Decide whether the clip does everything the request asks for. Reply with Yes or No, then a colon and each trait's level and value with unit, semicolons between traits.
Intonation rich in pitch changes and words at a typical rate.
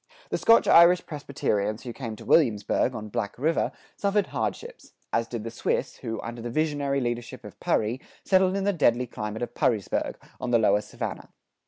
Yes: wide, 5.9 semitones; average, 180 wpm